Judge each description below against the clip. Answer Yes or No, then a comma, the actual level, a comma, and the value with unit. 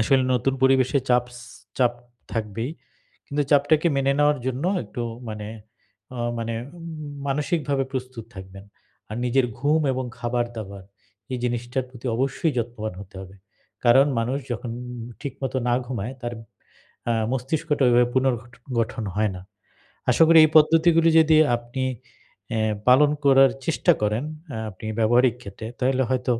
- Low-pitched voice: Yes, low, 125 Hz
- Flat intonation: No, average, 3.0 semitones